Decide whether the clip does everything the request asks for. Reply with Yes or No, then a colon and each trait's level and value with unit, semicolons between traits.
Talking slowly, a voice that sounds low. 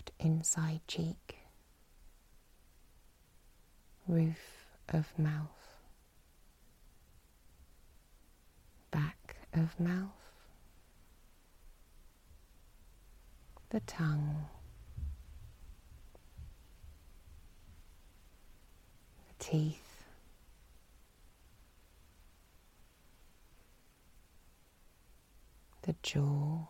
Yes: slow, 30 wpm; very low, 85 Hz